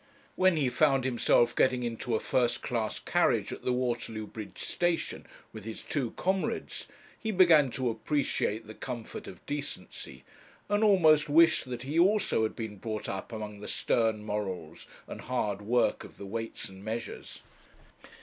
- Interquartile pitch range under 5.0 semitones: No, average, 5.3 semitones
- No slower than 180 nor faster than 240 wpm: No, average, 160 wpm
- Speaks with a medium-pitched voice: No, low, 120 Hz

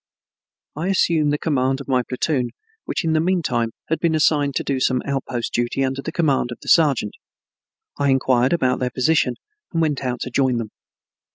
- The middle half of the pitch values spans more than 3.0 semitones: Yes, average, 3.7 semitones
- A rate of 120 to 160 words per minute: No, average, 195 wpm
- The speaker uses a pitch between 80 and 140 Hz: Yes, low, 135 Hz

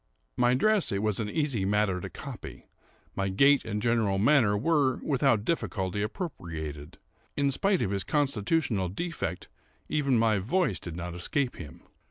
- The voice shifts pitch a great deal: Yes, wide, 6.6 semitones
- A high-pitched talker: No, low, 110 Hz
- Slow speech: No, average, 155 wpm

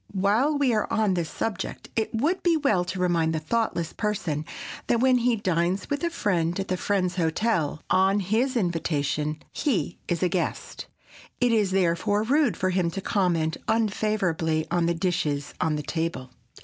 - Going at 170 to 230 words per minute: Yes, average, 175 wpm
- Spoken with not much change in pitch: No, average, 4.8 semitones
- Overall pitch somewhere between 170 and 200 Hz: Yes, medium, 185 Hz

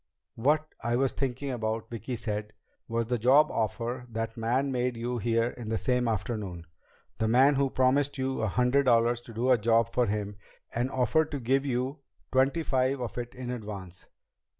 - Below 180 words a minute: No, average, 185 wpm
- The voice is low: Yes, low, 120 Hz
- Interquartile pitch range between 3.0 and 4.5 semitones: No, narrow, 2.5 semitones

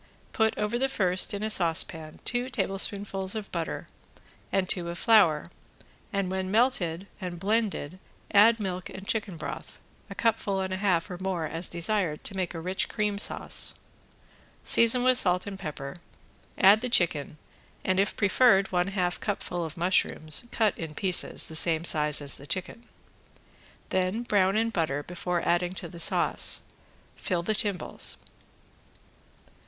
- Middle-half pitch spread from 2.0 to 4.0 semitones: Yes, average, 3.4 semitones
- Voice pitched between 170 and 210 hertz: Yes, medium, 185 Hz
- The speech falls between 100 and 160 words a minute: Yes, average, 155 wpm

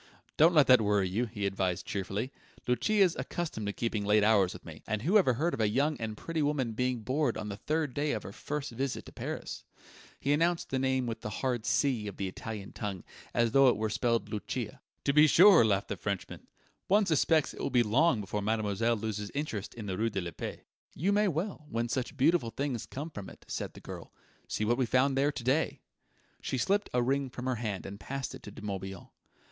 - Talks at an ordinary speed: No, fast, 225 wpm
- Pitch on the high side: No, low, 120 Hz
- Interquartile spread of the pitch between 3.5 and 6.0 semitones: Yes, wide, 5.5 semitones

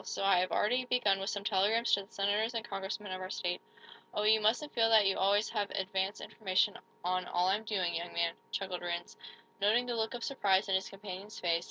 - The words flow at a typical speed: No, fast, 220 wpm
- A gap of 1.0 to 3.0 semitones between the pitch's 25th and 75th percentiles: Yes, average, 2.7 semitones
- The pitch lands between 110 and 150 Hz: No, high, 200 Hz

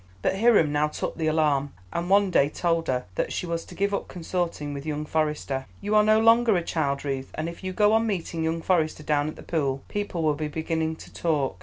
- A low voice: No, medium, 160 Hz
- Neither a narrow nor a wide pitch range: Yes, average, 3.9 semitones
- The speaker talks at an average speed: No, fast, 235 wpm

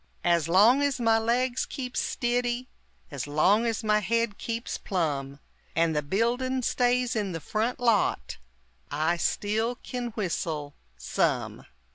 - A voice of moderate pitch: No, high, 220 Hz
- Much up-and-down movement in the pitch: Yes, wide, 6.4 semitones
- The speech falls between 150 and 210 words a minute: No, slow, 135 wpm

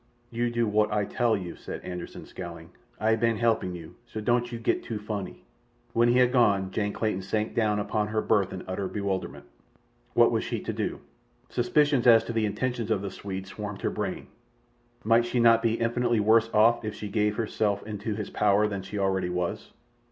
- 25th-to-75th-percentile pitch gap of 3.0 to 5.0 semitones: No, narrow, 2.6 semitones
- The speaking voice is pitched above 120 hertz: No, low, 105 Hz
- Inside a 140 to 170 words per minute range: No, average, 200 wpm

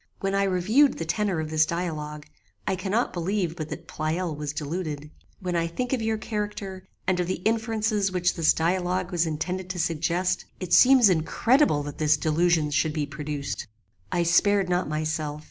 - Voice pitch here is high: No, medium, 175 Hz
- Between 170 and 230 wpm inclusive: Yes, average, 180 wpm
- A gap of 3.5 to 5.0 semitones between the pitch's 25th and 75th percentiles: Yes, average, 3.9 semitones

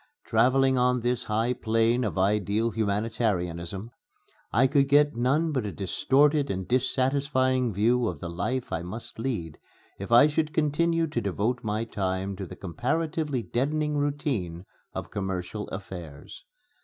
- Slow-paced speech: No, average, 145 wpm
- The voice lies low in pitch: Yes, low, 115 Hz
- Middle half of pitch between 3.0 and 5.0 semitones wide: No, wide, 5.4 semitones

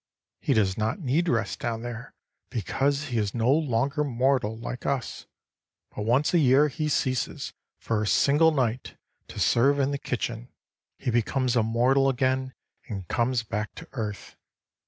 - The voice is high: No, low, 125 Hz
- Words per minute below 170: Yes, average, 160 wpm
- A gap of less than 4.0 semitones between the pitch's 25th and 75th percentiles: Yes, average, 3.4 semitones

